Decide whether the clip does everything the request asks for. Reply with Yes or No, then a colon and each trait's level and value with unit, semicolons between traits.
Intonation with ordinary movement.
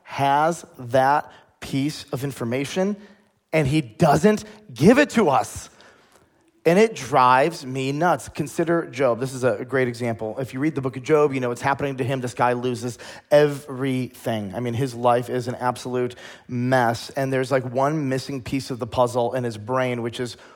Yes: average, 3.0 semitones